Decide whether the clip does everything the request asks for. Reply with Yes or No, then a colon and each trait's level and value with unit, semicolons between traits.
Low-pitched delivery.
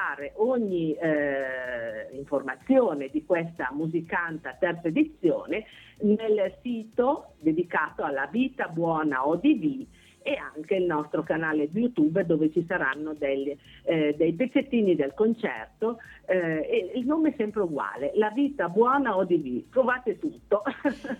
No: high, 195 Hz